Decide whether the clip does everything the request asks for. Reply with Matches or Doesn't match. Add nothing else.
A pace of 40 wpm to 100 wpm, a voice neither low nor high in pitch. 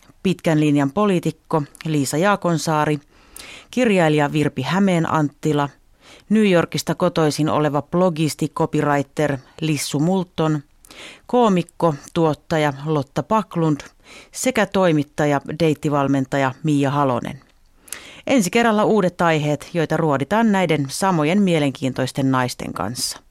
Matches